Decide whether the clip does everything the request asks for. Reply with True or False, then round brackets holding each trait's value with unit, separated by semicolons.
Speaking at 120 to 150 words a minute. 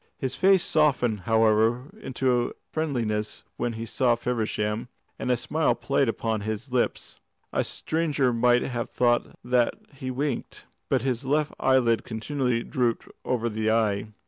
True (145 wpm)